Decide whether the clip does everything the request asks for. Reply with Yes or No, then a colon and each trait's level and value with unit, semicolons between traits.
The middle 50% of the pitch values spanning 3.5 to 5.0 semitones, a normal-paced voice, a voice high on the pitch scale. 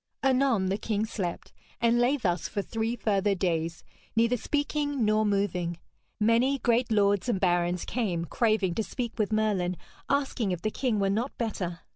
Yes: average, 4.2 semitones; average, 165 wpm; high, 215 Hz